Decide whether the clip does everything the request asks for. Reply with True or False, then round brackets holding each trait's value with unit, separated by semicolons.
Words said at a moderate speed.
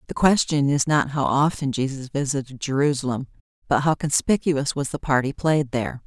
True (180 wpm)